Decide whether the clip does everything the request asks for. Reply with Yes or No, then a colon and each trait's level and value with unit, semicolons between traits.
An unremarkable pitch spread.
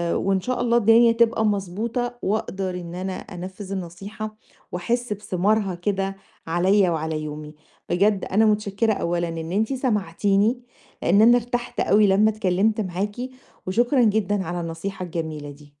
Yes: average, 3.8 semitones